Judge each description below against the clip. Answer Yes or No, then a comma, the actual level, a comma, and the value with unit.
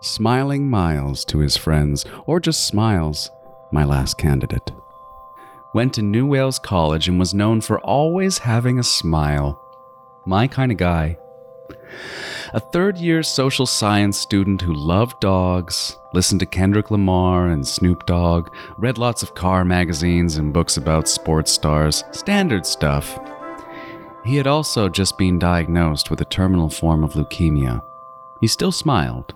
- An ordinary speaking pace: Yes, average, 145 wpm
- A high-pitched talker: No, very low, 95 Hz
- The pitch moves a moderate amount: No, wide, 8.2 semitones